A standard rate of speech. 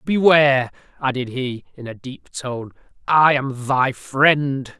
No: slow, 125 wpm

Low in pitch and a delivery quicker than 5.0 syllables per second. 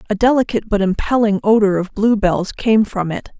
No: high, 210 Hz; 5.5 syllables/s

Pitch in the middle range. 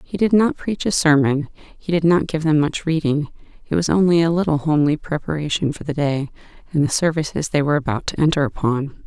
Yes: medium, 155 Hz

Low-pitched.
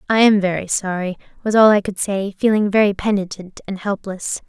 No: high, 200 Hz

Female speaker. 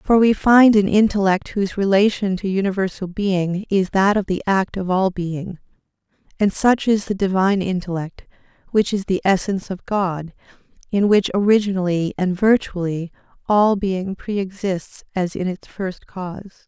Yes: female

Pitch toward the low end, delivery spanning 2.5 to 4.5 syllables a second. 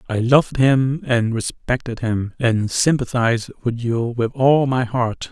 Yes: low, 120 Hz; 4.1 syllables/s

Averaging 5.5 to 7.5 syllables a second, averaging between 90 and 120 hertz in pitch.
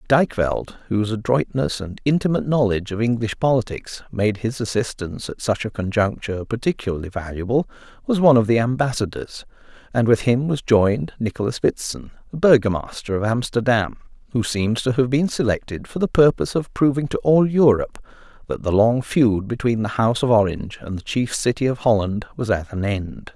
Yes: 5.6 syllables/s; low, 115 Hz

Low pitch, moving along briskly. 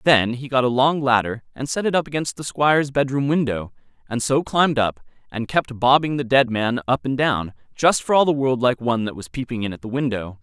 Yes: low, 130 Hz; fast, 240 wpm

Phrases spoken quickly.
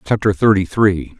No: average, 150 wpm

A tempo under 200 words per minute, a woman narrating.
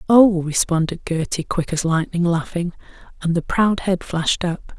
Yes: average, 165 wpm; female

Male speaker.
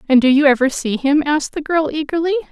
No: female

